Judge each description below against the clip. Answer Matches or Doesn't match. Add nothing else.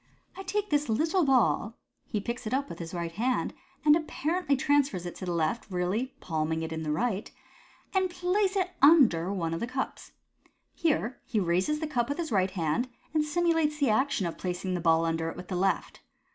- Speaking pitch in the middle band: Doesn't match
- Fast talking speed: Matches